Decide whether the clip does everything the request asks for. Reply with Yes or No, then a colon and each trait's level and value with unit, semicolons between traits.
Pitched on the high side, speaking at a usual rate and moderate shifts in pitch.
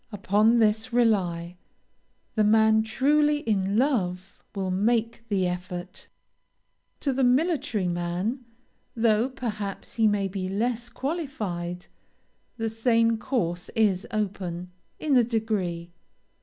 No: high, 215 Hz; slow, 115 wpm; average, 4.4 semitones